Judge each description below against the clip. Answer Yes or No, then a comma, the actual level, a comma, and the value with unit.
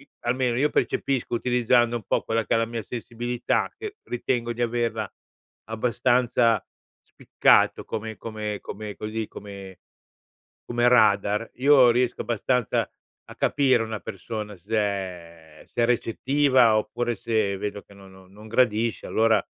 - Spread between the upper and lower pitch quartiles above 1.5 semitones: Yes, narrow, 2.6 semitones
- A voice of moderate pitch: No, low, 115 Hz